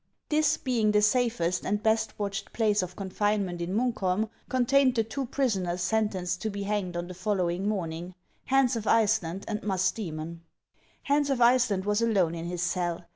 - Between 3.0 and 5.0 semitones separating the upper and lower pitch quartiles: Yes, average, 4.0 semitones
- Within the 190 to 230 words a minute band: No, average, 175 wpm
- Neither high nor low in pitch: No, high, 205 Hz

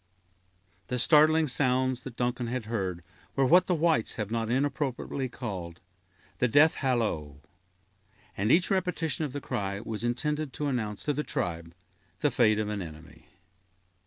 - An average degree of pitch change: No, wide, 5.7 semitones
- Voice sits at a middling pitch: No, low, 125 Hz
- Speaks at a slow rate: No, average, 155 wpm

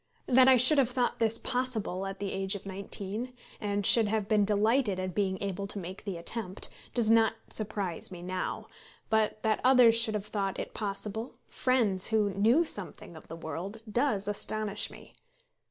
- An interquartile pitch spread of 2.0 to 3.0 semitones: Yes, average, 2.7 semitones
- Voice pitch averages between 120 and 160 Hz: No, high, 210 Hz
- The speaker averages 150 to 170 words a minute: No, average, 180 wpm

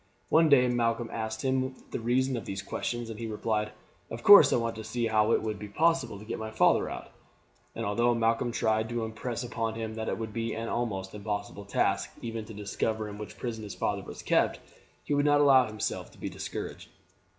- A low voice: Yes, low, 115 Hz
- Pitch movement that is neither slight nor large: No, narrow, 1.9 semitones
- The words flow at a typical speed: No, fast, 215 wpm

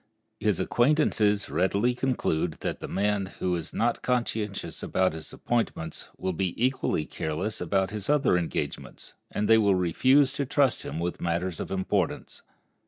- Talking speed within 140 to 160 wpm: Yes, average, 155 wpm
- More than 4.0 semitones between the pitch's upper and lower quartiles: Yes, average, 5.2 semitones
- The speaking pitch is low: Yes, low, 100 Hz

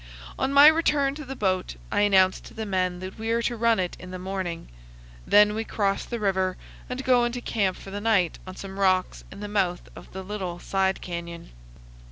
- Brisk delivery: Yes, fast, 215 wpm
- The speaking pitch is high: Yes, high, 195 Hz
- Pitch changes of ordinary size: Yes, average, 3.5 semitones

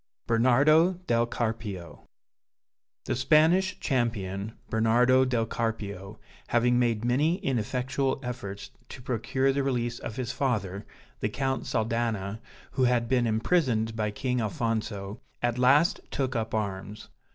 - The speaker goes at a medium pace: No, slow, 125 wpm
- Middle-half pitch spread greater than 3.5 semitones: No, average, 3.0 semitones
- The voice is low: Yes, low, 120 Hz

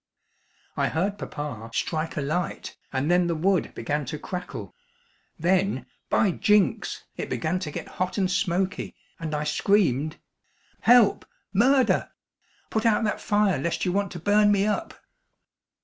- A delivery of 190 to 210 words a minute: No, average, 150 wpm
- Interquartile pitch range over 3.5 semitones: Yes, average, 4.9 semitones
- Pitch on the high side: No, medium, 180 Hz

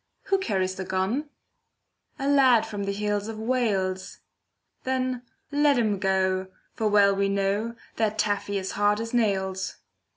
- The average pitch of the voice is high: Yes, high, 205 Hz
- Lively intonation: No, average, 3.4 semitones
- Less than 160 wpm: Yes, average, 150 wpm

